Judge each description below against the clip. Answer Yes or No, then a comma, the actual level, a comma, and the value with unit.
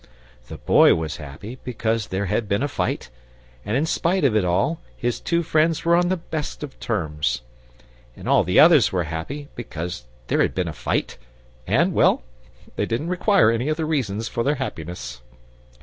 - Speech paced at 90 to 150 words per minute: No, average, 180 wpm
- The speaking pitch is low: Yes, low, 115 Hz